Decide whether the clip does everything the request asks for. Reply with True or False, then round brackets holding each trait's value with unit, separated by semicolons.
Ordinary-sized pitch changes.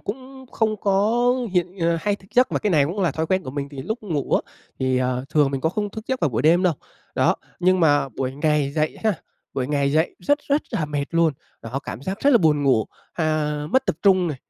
False (6.1 semitones)